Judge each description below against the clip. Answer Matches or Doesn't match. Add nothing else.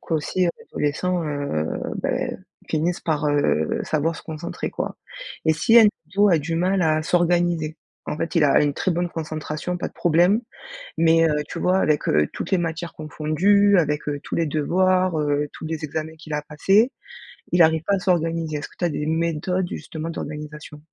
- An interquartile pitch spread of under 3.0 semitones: Matches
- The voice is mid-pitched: Matches